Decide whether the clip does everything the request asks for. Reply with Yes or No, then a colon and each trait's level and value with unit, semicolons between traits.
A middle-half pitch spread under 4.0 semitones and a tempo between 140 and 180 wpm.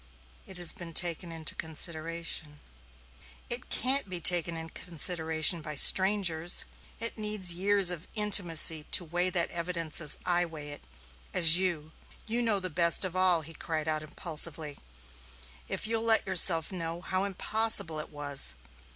Yes: average, 2.7 semitones; average, 150 wpm